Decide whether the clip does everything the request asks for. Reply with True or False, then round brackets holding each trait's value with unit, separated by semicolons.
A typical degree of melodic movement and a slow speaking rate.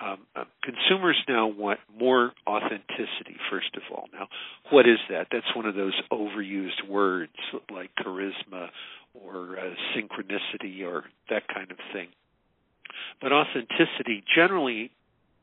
False (2.3 semitones; 125 wpm)